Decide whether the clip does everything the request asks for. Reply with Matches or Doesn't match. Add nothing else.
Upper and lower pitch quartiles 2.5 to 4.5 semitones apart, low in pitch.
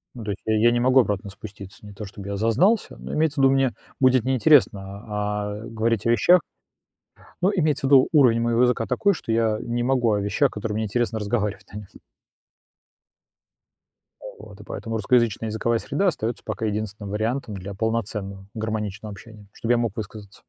Matches